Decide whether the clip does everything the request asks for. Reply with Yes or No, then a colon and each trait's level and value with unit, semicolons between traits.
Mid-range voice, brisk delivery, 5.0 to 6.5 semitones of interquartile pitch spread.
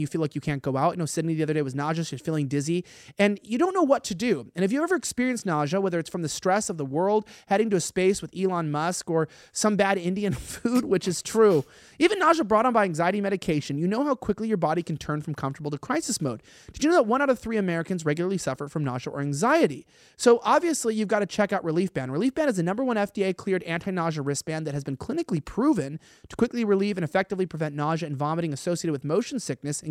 Yes: medium, 180 Hz; fast, 255 wpm; wide, 5.5 semitones